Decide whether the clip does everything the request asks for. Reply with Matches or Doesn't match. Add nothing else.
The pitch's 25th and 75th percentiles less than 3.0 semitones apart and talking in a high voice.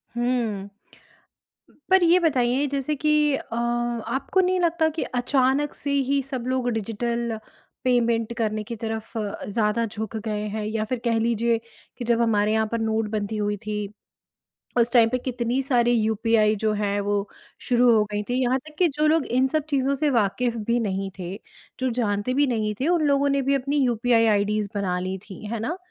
Doesn't match